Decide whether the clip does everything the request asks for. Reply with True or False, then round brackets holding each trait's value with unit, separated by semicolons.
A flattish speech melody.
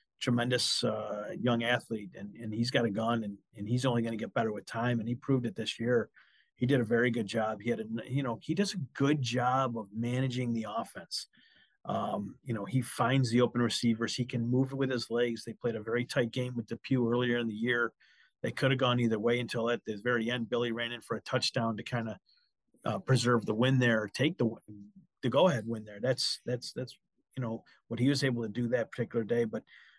True (1.7 semitones)